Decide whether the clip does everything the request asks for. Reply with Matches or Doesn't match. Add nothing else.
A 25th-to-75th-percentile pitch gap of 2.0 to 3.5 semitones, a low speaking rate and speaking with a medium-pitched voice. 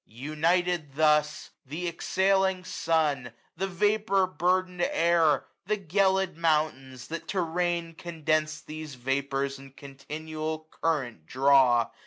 Doesn't match